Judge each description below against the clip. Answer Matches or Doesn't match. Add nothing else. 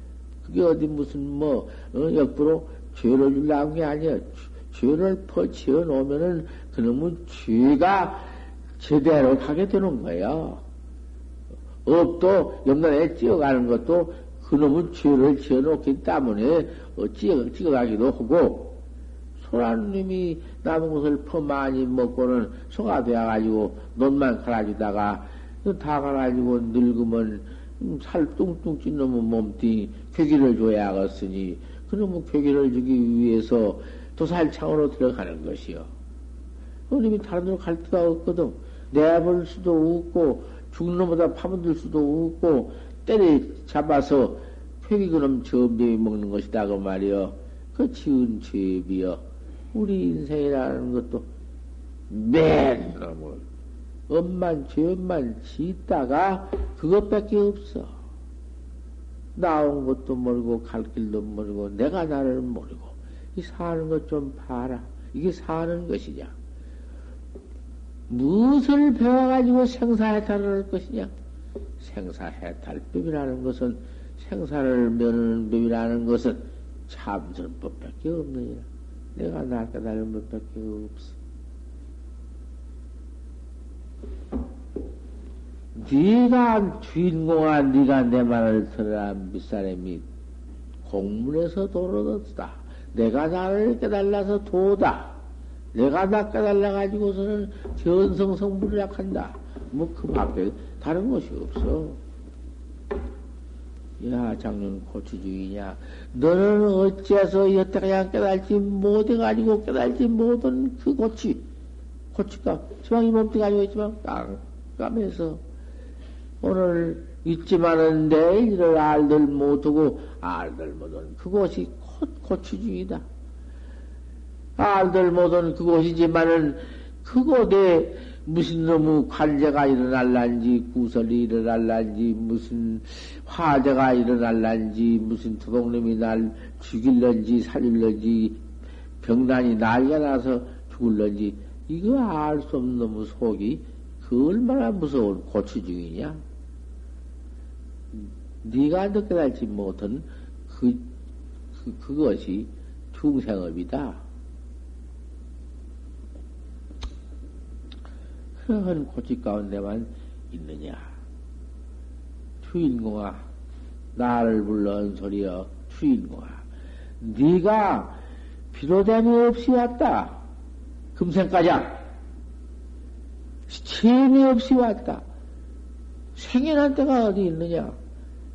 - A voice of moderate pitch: Doesn't match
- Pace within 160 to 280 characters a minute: Matches